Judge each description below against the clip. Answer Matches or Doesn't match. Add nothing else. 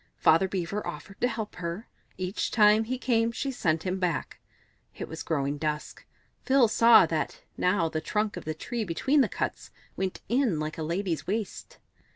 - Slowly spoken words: Doesn't match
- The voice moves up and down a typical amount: Doesn't match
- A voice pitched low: Doesn't match